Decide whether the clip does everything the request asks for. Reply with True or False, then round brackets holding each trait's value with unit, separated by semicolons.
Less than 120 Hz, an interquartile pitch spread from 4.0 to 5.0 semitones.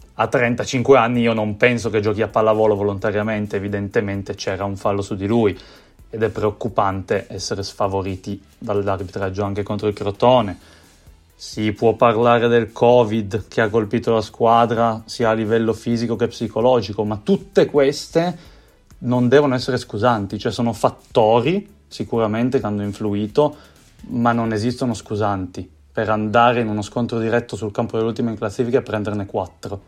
False (110 Hz; 2.6 semitones)